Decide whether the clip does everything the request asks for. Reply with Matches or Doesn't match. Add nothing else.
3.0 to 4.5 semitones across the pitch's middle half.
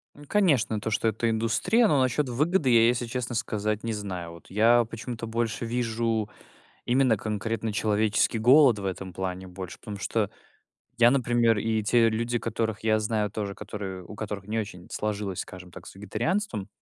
Doesn't match